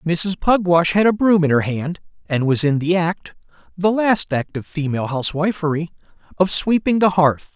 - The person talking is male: Yes, male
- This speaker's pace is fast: No, average, 185 wpm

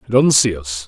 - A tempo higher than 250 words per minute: Yes, fast, 275 wpm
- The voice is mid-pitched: No, low, 110 Hz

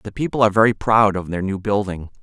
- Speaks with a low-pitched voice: Yes, low, 100 Hz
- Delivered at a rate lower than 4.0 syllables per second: No, 6.2 syllables/s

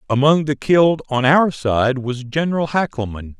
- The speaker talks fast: No, average, 160 wpm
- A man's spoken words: Yes, male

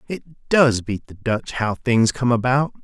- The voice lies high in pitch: No, low, 120 Hz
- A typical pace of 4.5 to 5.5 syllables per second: No, 3.9 syllables/s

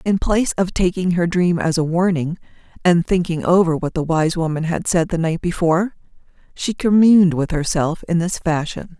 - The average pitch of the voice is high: No, medium, 170 Hz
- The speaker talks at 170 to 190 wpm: Yes, average, 185 wpm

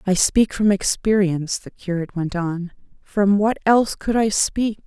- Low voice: No, high, 195 Hz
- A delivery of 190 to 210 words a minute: No, average, 160 wpm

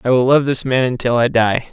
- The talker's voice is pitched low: Yes, low, 125 Hz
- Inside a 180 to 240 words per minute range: No, fast, 280 wpm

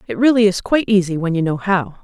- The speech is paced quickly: Yes, fast, 265 wpm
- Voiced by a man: No, female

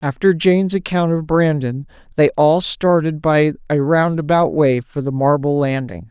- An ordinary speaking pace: Yes, average, 155 wpm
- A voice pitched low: No, medium, 150 Hz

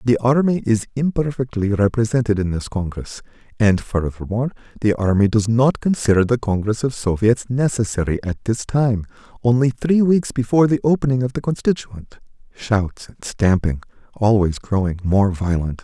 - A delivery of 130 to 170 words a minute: Yes, average, 150 wpm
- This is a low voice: Yes, low, 115 Hz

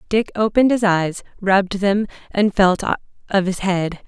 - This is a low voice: No, high, 195 Hz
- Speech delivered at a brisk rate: No, average, 160 wpm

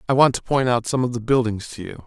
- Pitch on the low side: Yes, low, 120 Hz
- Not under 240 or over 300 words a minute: No, fast, 320 wpm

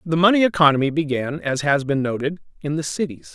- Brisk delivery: No, average, 195 wpm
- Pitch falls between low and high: Yes, medium, 150 Hz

